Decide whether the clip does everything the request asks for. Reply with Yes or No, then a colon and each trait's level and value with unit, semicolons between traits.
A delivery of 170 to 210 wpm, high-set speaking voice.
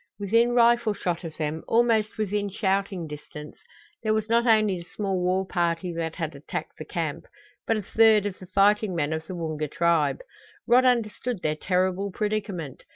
Yes: average, 175 wpm; high, 195 Hz